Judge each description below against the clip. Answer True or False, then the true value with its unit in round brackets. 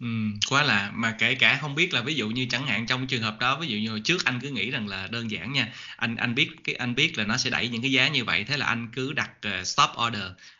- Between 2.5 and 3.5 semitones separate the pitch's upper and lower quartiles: True (3.2 semitones)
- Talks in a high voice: False (120 Hz)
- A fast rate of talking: True (300 wpm)